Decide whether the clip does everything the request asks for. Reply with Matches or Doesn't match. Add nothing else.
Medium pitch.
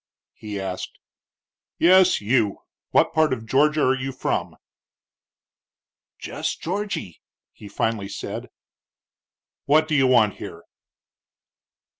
Doesn't match